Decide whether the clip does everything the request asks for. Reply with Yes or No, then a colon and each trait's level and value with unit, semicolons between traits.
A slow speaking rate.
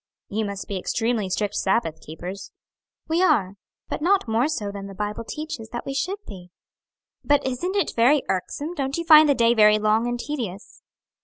No: average, 185 wpm